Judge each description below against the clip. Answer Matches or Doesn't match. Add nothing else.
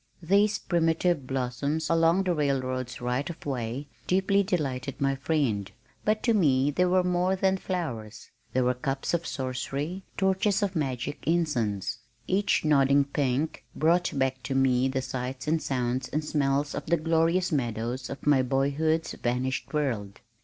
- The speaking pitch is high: Doesn't match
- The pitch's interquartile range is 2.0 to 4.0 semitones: Doesn't match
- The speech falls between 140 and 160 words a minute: Matches